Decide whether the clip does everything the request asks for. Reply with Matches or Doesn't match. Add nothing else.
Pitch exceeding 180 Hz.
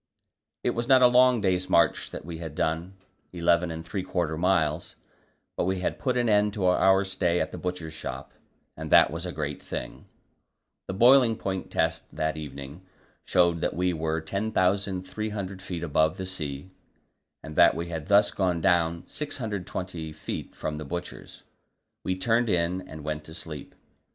Doesn't match